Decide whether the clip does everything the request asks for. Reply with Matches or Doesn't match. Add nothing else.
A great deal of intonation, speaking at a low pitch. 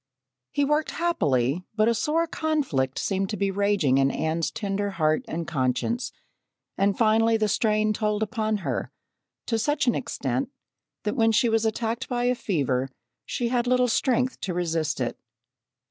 Doesn't match